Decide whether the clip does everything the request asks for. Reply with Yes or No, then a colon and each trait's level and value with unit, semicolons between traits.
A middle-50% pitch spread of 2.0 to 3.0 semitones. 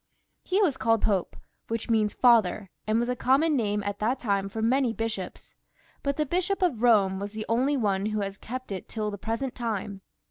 No: average, 3.9 semitones